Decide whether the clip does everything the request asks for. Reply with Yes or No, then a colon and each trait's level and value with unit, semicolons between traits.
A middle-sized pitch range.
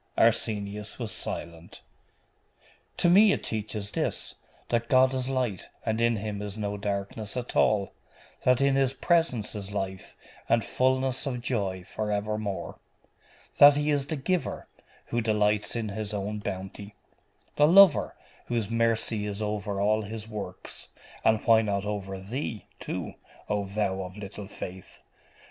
Yes: average, 3.3 semitones